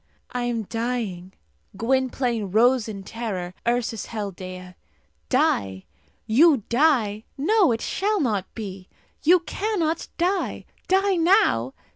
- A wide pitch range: Yes, wide, 7.9 semitones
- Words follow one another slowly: Yes, slow, 115 wpm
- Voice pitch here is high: Yes, high, 235 Hz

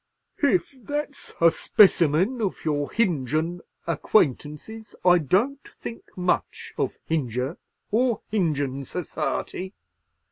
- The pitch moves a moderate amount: No, wide, 6.9 semitones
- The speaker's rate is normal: No, slow, 100 wpm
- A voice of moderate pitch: Yes, medium, 180 Hz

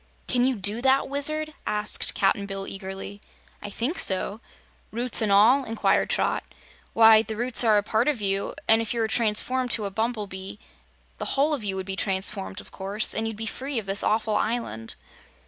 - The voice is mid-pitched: No, high, 220 Hz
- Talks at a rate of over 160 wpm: Yes, average, 200 wpm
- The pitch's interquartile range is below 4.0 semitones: Yes, average, 3.4 semitones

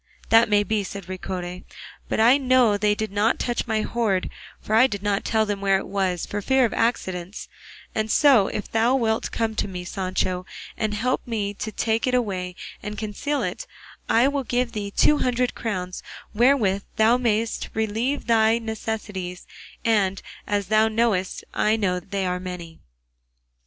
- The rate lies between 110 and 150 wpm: No, average, 170 wpm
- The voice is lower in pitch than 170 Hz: No, high, 215 Hz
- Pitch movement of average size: Yes, average, 3.1 semitones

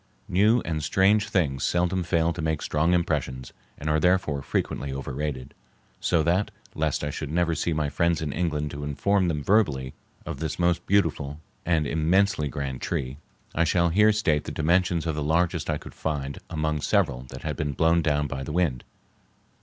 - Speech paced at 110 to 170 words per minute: No, average, 185 wpm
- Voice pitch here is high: No, very low, 80 Hz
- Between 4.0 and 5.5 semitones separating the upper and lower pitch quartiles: No, average, 3.3 semitones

